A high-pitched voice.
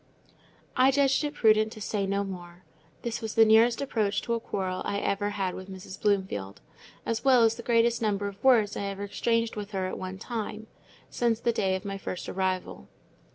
Yes: high, 205 Hz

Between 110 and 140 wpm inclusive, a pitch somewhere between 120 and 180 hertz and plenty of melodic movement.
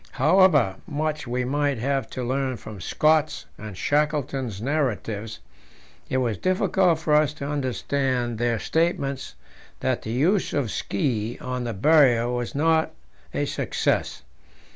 No: slow, 135 wpm; low, 135 Hz; average, 4.1 semitones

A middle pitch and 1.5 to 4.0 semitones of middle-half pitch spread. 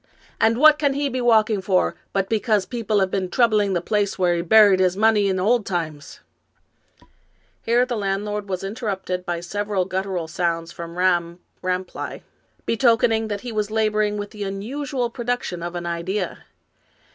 No: high, 205 Hz; average, 3.4 semitones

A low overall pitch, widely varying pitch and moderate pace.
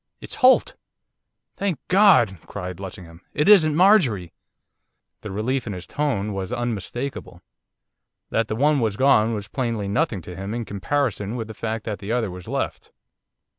Yes: low, 115 Hz; wide, 6.0 semitones; average, 160 wpm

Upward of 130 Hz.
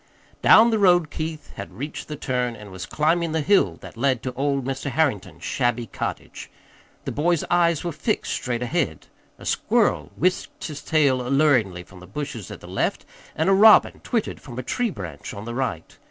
Yes: medium, 140 Hz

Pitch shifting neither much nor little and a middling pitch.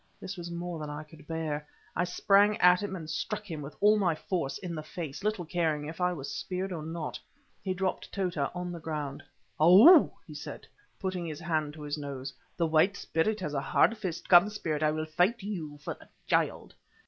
Yes: average, 3.6 semitones; medium, 170 Hz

